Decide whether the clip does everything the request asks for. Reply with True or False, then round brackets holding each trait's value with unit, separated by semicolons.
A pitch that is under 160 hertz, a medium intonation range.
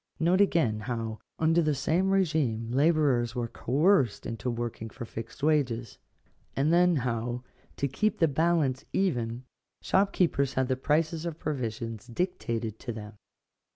False (135 Hz; 5.9 semitones)